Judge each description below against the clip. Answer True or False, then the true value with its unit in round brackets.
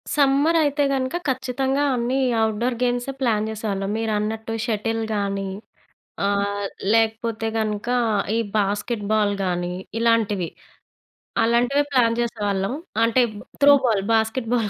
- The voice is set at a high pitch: True (225 Hz)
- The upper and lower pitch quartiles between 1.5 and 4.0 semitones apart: True (3.0 semitones)